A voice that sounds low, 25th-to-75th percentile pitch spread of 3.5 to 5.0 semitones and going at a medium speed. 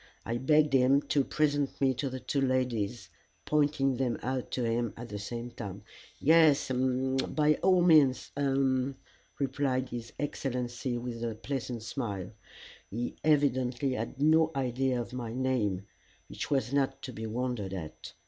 No: low, 130 Hz; average, 2.7 semitones; average, 155 wpm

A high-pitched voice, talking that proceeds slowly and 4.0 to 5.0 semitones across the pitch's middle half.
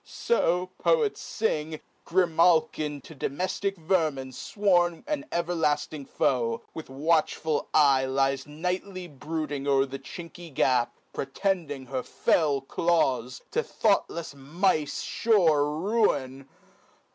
No: medium, 155 Hz; slow, 105 wpm; average, 4.5 semitones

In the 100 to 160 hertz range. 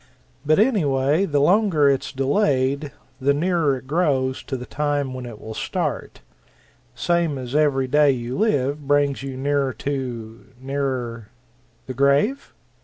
Yes: medium, 140 Hz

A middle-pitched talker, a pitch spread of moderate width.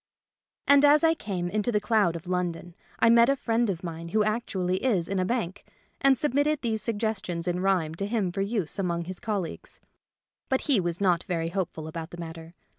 No: high, 195 Hz; average, 4.9 semitones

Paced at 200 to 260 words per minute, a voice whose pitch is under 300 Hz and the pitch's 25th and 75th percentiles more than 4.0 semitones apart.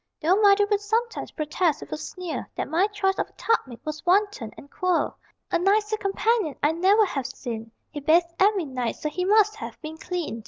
No: fast, 205 wpm; very high, 360 Hz; average, 5.2 semitones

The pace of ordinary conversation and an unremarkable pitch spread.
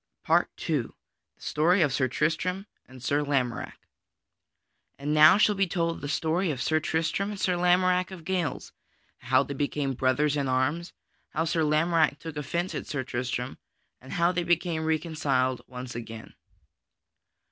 Yes: average, 155 wpm; average, 4.2 semitones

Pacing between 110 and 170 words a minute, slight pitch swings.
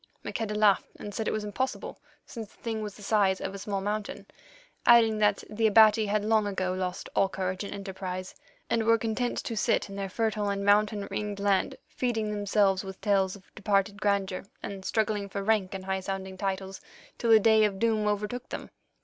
No: average, 200 wpm; narrow, 1.9 semitones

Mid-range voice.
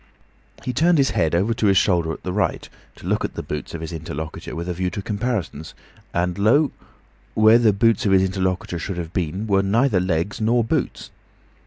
No: very low, 95 Hz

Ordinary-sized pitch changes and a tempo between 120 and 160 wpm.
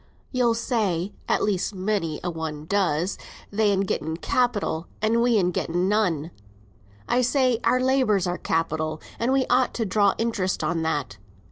No: wide, 5.8 semitones; average, 150 wpm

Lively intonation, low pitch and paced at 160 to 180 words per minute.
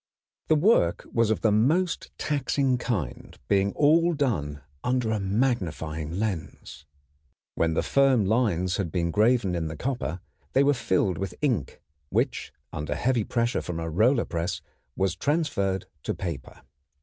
No: wide, 7.2 semitones; low, 105 Hz; average, 150 wpm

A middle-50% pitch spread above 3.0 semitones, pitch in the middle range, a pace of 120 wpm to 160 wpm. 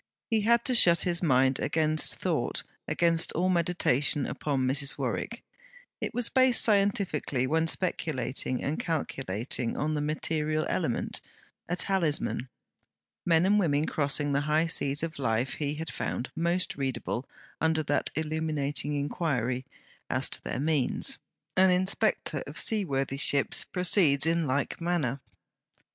Yes: average, 3.7 semitones; medium, 155 Hz; average, 140 wpm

